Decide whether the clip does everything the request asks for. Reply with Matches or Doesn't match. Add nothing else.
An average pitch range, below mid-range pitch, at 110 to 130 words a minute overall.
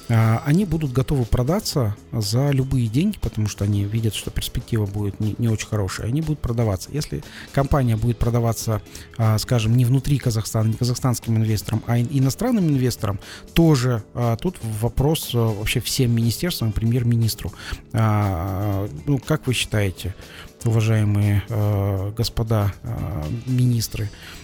Matches